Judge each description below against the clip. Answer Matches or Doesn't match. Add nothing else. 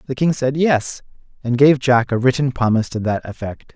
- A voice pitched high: Doesn't match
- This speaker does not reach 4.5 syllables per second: Doesn't match